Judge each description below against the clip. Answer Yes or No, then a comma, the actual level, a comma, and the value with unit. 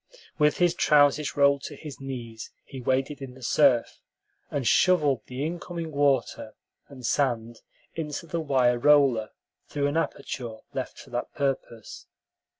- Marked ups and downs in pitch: No, average, 3.0 semitones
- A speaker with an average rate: Yes, average, 145 wpm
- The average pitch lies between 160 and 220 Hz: No, medium, 140 Hz